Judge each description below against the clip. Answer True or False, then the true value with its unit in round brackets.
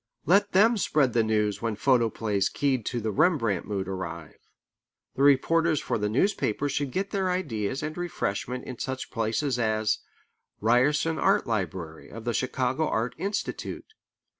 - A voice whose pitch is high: False (125 Hz)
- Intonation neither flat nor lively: False (5.9 semitones)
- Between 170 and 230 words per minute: False (155 wpm)